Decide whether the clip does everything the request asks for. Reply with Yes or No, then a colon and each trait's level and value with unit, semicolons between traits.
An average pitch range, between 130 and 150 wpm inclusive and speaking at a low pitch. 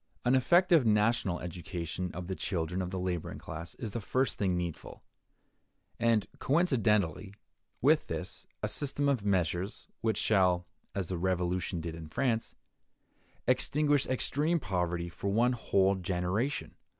No: wide, 5.7 semitones; average, 140 wpm; very low, 95 Hz